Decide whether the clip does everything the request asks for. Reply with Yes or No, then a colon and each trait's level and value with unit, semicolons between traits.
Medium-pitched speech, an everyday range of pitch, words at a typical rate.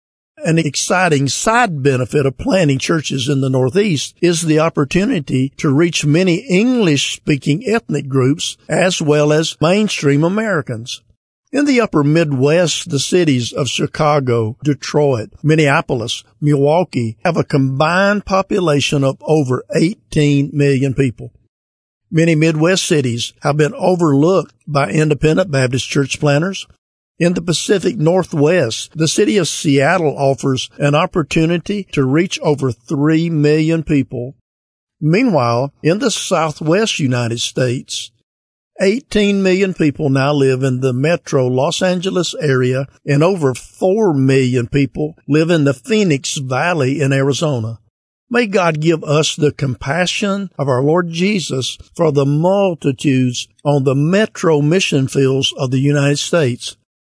No: medium, 150 Hz; average, 4.1 semitones; slow, 130 wpm